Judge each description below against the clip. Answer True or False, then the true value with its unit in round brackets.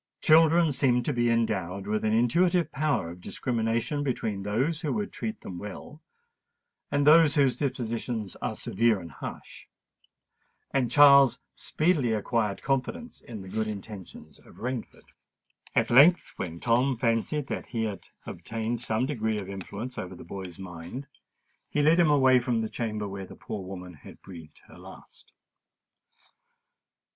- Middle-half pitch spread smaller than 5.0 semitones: False (5.3 semitones)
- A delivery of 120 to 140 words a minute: False (150 wpm)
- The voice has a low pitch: True (115 Hz)